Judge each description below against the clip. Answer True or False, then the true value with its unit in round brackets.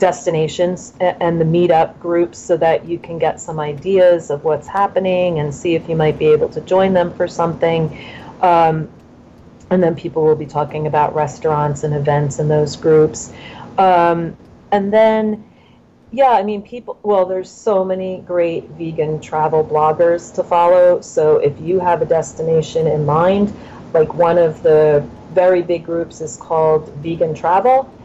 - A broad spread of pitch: False (2.8 semitones)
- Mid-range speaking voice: True (170 Hz)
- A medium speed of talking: True (165 wpm)